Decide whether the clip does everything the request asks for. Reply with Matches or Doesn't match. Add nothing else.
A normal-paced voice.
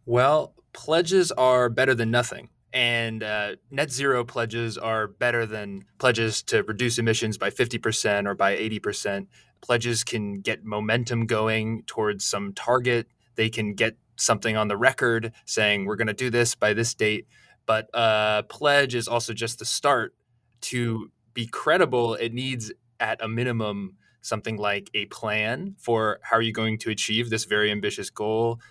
Matches